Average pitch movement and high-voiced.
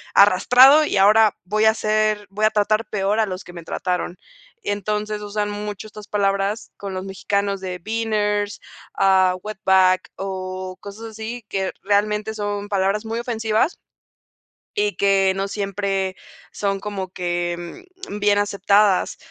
No: narrow, 1.9 semitones; high, 205 Hz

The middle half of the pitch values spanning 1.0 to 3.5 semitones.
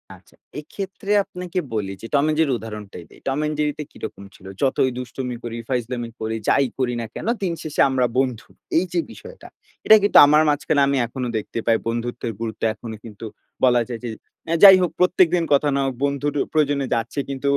No: average, 4.5 semitones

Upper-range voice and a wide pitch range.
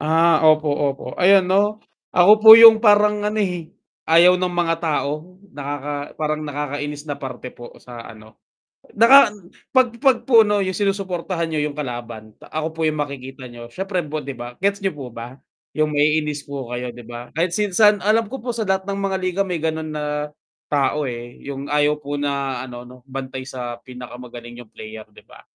No: medium, 150 Hz; wide, 6.2 semitones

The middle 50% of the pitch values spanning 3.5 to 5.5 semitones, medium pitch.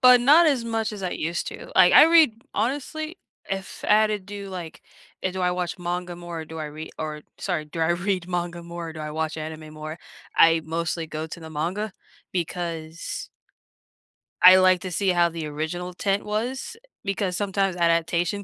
Yes: average, 3.8 semitones; medium, 175 Hz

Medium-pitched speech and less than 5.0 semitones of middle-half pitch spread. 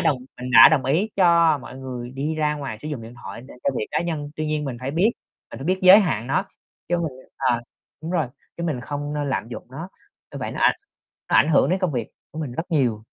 Yes: medium, 145 Hz; average, 4.1 semitones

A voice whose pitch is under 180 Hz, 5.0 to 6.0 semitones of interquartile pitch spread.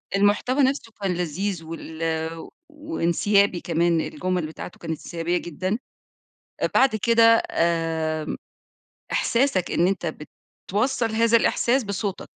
No: medium, 185 Hz; wide, 5.5 semitones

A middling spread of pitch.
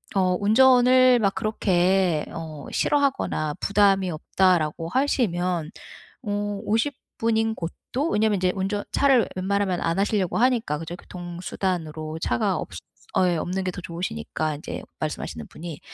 Yes: average, 4.6 semitones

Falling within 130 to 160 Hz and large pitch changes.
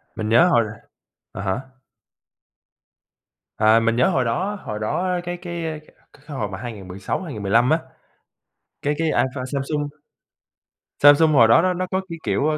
Yes: low, 135 Hz; wide, 6.8 semitones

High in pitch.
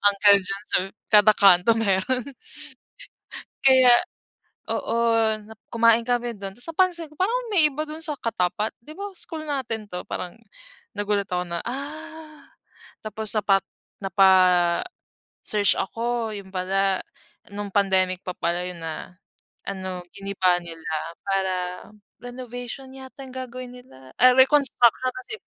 Yes: high, 220 Hz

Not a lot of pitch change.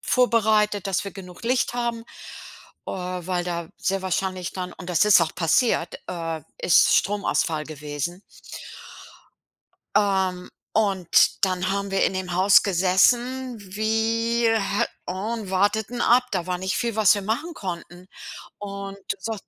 No: average, 3.4 semitones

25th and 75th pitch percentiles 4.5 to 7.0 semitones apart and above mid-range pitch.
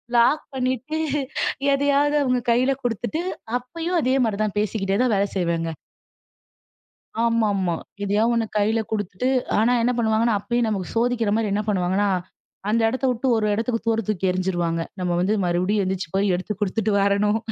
No: average, 3.8 semitones; high, 220 Hz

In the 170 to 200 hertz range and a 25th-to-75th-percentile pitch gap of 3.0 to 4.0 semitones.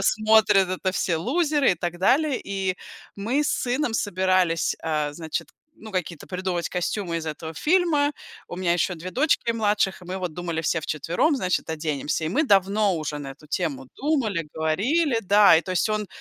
No: medium, 185 Hz; average, 5.0 semitones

